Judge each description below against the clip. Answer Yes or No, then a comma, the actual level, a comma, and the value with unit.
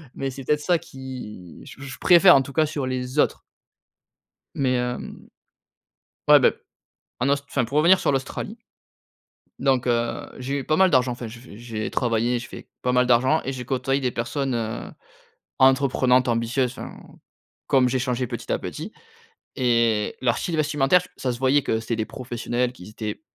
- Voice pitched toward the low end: Yes, low, 130 Hz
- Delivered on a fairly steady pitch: Yes, narrow, 2.3 semitones